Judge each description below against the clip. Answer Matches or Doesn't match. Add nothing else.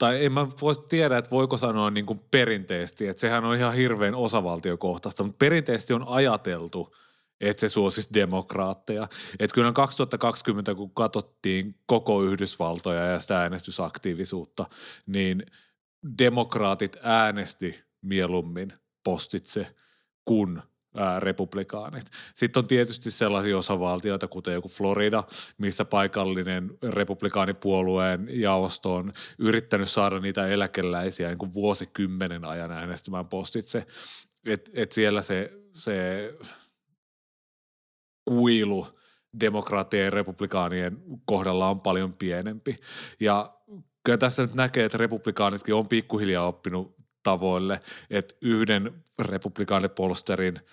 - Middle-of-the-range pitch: Doesn't match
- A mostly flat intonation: Doesn't match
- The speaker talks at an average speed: Matches